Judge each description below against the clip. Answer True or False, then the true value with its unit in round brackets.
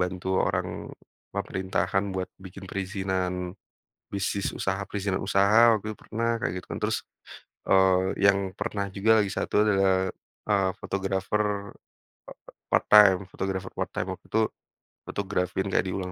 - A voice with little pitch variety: True (1.2 semitones)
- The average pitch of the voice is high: False (95 Hz)